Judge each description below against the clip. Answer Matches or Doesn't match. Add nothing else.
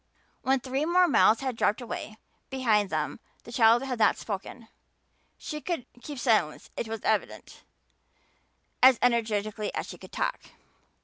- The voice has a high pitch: Matches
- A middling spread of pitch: Matches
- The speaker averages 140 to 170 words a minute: Matches